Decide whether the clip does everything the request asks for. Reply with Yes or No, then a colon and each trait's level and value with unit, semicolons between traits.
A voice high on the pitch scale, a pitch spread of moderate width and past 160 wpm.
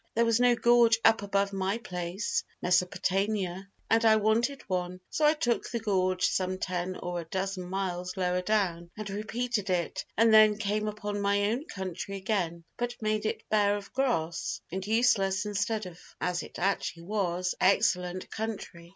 Yes: high, 200 Hz; average, 3.1 semitones; average, 170 wpm